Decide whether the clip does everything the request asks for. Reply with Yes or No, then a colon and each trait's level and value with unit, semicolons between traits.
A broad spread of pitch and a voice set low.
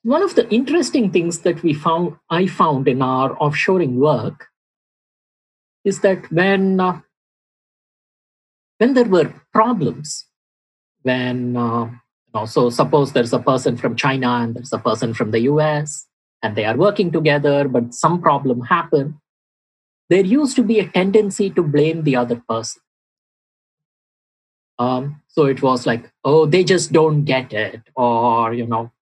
No: wide, 6.8 semitones; medium, 150 Hz